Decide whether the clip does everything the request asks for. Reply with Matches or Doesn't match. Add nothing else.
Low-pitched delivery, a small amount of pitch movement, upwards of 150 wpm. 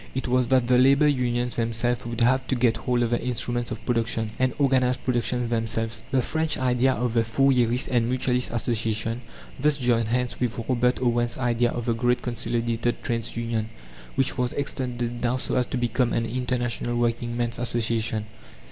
Matches